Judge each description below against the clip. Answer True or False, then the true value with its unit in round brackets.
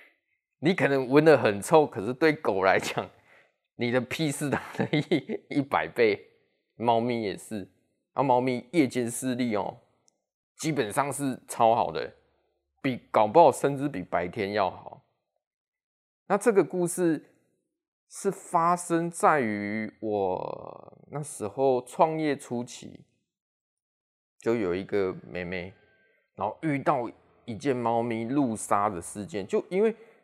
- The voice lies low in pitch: True (130 Hz)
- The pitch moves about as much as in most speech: False (6.6 semitones)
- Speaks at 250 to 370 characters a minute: False (185 characters per minute)